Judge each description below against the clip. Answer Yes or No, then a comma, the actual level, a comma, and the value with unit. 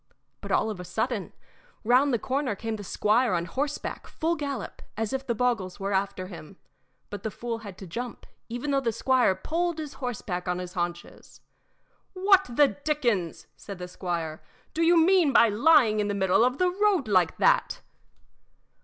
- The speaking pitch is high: Yes, high, 230 Hz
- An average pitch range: No, wide, 6.9 semitones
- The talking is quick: No, average, 185 wpm